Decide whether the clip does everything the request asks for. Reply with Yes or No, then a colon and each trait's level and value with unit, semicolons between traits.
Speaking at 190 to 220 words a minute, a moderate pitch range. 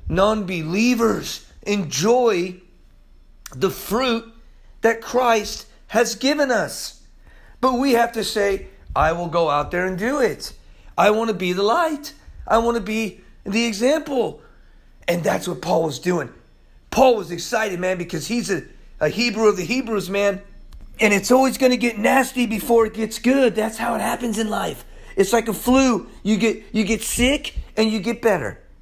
No: average, 175 wpm; average, 3.6 semitones